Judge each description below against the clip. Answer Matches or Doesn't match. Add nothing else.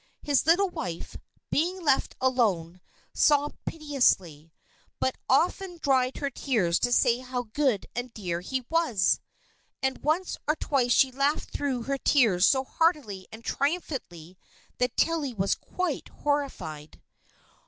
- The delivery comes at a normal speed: Doesn't match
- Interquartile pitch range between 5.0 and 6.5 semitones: Matches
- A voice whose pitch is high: Matches